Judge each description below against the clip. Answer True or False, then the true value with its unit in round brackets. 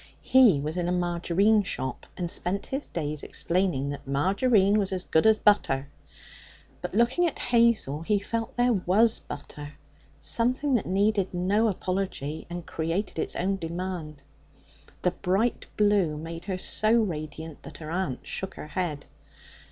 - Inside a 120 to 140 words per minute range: False (155 wpm)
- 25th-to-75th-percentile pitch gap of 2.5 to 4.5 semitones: False (4.9 semitones)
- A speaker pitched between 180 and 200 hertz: True (185 Hz)